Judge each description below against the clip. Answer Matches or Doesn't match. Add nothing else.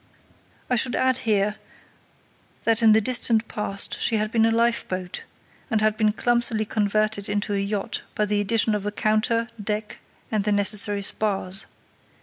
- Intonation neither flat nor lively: Doesn't match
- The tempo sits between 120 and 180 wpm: Matches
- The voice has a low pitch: Doesn't match